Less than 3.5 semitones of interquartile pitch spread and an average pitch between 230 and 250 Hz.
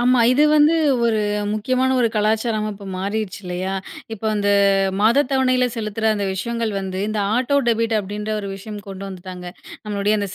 No: average, 2.9 semitones; high, 215 Hz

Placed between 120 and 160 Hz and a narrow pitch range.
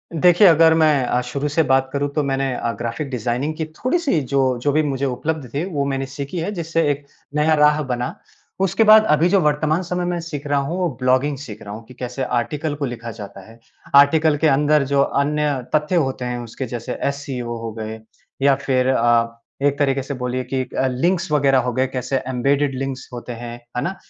No: medium, 140 Hz; average, 3.5 semitones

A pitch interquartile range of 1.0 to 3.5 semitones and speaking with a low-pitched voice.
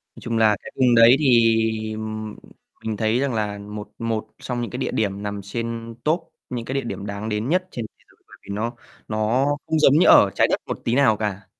Yes: average, 3.0 semitones; low, 115 Hz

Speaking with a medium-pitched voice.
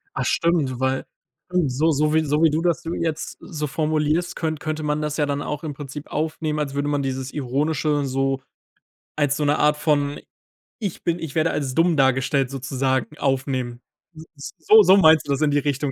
Yes: medium, 150 Hz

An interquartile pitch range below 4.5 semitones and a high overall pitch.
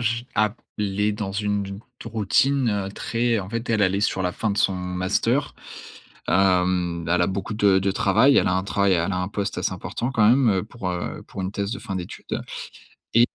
No: average, 2.9 semitones; low, 100 Hz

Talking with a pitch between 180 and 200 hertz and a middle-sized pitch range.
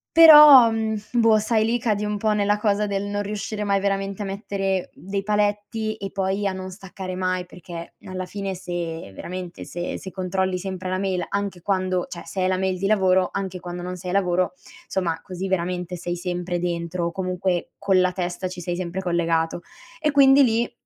No: high, 190 Hz; narrow, 2.3 semitones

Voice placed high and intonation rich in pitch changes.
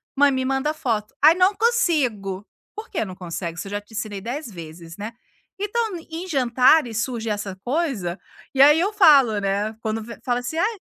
Yes: high, 245 Hz; wide, 7.6 semitones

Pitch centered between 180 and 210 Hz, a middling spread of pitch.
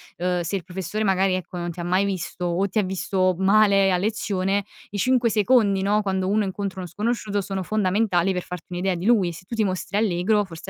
No: high, 190 Hz; narrow, 2.3 semitones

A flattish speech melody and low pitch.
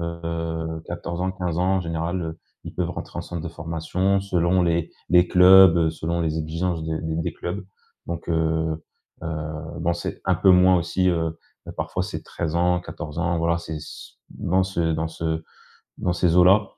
Yes: narrow, 1.7 semitones; very low, 85 Hz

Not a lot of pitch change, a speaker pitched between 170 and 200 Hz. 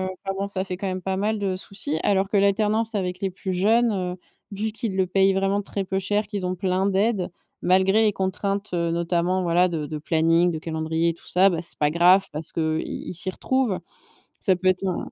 Yes: narrow, 2.2 semitones; high, 190 Hz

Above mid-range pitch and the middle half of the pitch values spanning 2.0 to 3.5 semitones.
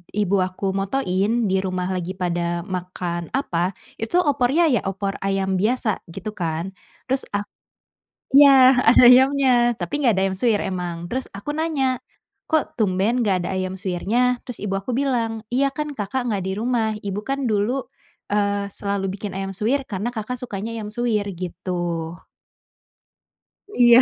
No: high, 210 Hz; average, 4.7 semitones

